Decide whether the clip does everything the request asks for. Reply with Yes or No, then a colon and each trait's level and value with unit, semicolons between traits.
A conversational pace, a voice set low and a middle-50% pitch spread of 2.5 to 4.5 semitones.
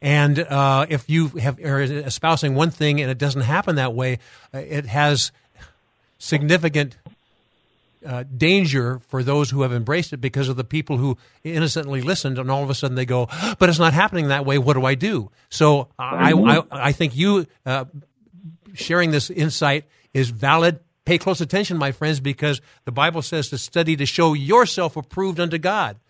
No: average, 180 wpm; medium, 145 Hz; average, 3.5 semitones